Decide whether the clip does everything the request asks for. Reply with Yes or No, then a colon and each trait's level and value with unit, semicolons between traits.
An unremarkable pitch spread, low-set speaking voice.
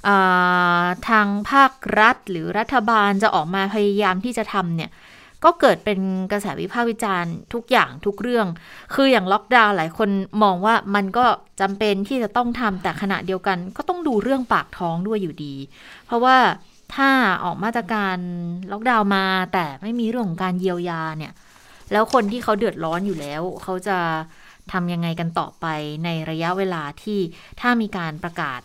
No: average, 4.2 semitones; high, 195 Hz